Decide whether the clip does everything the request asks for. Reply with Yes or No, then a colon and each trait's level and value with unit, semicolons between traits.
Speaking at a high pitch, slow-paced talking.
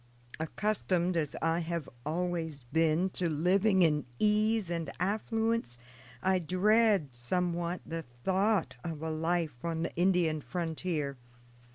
No: medium, 170 Hz; slow, 125 wpm